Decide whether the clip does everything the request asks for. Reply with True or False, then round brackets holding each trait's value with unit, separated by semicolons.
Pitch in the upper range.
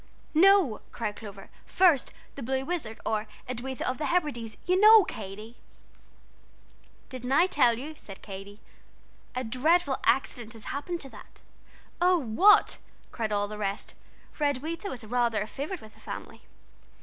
True (255 Hz)